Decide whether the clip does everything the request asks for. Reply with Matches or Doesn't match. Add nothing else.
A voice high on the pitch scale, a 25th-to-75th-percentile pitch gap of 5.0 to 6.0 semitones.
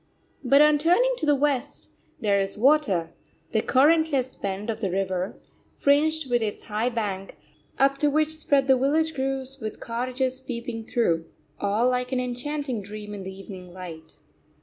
Matches